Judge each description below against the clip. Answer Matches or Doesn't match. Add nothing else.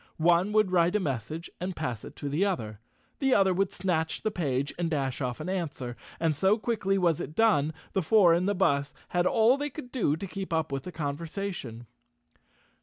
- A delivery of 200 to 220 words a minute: Matches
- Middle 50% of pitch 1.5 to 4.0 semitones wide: Doesn't match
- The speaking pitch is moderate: Matches